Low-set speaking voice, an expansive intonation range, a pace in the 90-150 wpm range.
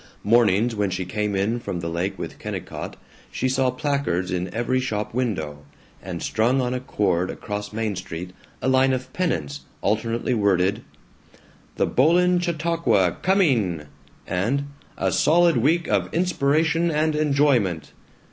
Yes: low, 115 Hz; wide, 6.8 semitones; average, 140 wpm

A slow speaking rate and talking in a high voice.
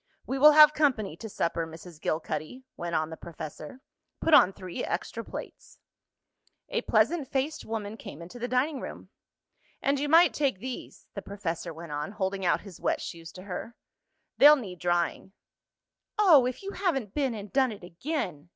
No: average, 175 wpm; high, 210 Hz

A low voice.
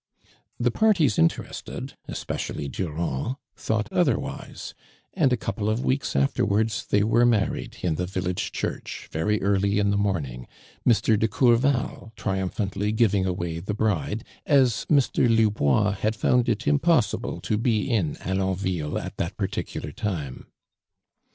Yes: low, 105 Hz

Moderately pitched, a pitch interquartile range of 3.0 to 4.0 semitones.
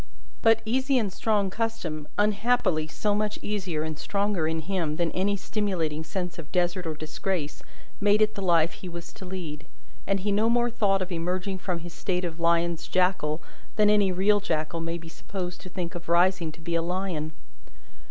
Yes: medium, 180 Hz; average, 3.5 semitones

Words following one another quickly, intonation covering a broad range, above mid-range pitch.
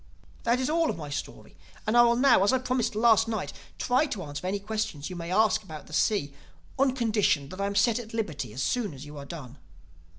Yes: fast, 235 wpm; wide, 7.4 semitones; high, 210 Hz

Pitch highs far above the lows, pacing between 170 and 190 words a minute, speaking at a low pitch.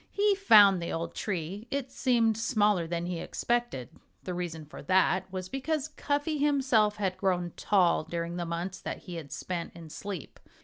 No: wide, 5.9 semitones; average, 175 wpm; high, 190 Hz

